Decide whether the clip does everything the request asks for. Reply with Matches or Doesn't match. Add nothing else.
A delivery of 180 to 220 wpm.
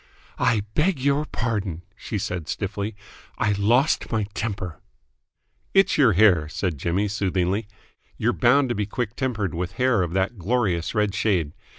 Doesn't match